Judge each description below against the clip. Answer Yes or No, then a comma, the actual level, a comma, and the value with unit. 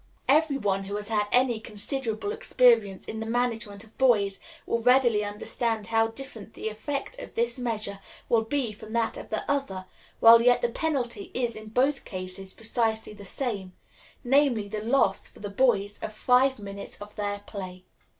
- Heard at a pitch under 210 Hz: No, high, 225 Hz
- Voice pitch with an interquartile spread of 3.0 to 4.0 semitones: Yes, average, 3.4 semitones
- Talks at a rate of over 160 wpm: Yes, average, 175 wpm